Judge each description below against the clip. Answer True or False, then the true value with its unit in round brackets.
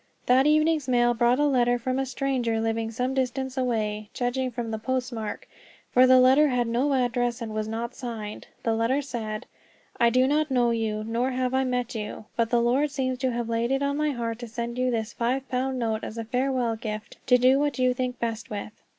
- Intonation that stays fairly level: True (2.2 semitones)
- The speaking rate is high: True (220 wpm)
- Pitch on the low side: False (245 Hz)